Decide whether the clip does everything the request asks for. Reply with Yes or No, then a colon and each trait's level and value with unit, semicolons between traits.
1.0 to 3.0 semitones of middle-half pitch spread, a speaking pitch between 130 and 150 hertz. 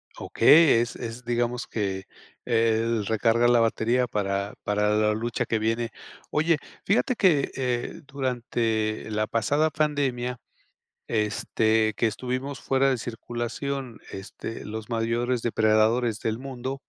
No: narrow, 2.5 semitones; low, 115 Hz